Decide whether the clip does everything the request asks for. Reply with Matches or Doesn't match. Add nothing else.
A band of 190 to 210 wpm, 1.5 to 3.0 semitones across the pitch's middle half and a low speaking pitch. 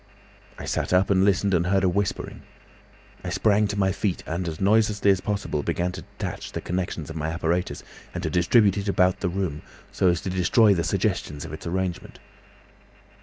Matches